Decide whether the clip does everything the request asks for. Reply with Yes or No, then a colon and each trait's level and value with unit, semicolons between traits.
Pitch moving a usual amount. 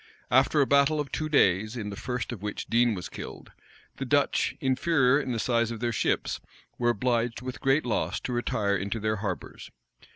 Yes: average, 3.6 semitones